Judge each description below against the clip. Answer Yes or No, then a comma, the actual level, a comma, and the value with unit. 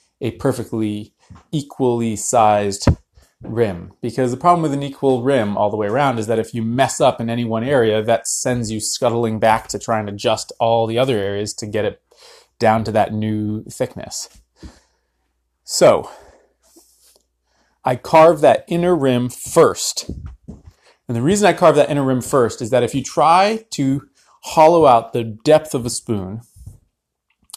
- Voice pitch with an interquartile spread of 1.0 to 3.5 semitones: No, average, 4.2 semitones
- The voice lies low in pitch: Yes, low, 115 Hz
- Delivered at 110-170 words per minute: Yes, average, 165 wpm